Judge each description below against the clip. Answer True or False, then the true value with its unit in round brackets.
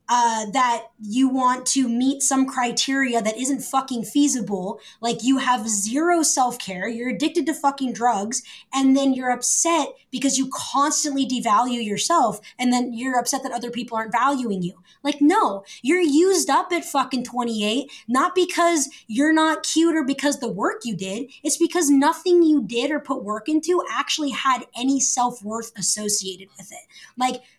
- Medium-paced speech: True (170 wpm)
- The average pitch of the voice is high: True (260 Hz)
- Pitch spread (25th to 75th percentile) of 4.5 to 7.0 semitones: False (3.7 semitones)